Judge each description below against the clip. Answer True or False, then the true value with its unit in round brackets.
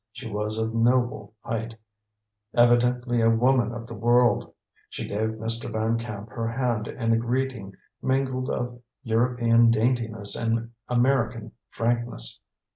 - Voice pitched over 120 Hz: False (115 Hz)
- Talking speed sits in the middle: False (130 wpm)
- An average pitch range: False (1.5 semitones)